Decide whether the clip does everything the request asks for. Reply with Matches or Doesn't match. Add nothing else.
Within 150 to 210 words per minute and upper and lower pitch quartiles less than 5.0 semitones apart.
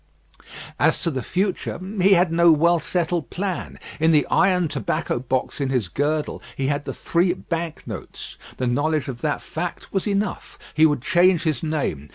Matches